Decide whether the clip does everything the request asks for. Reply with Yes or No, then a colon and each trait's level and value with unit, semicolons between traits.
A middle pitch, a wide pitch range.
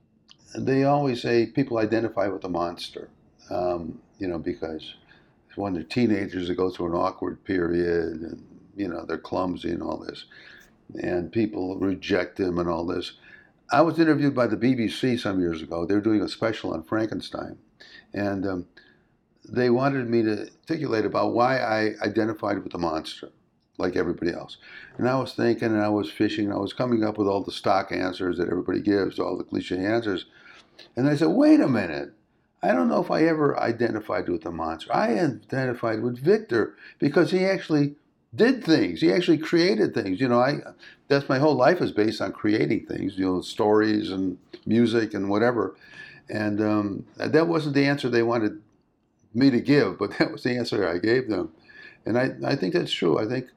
No: low, 115 Hz; wide, 5.7 semitones